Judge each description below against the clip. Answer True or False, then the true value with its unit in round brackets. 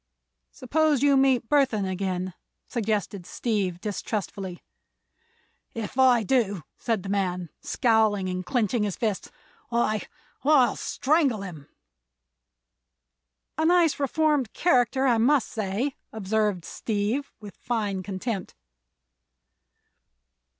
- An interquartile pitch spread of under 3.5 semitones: False (5.1 semitones)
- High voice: True (220 Hz)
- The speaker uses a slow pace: True (100 wpm)